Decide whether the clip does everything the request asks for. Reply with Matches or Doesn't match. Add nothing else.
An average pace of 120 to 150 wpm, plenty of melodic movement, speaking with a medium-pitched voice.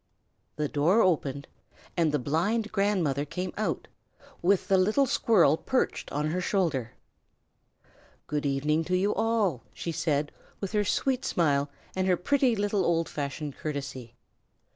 Matches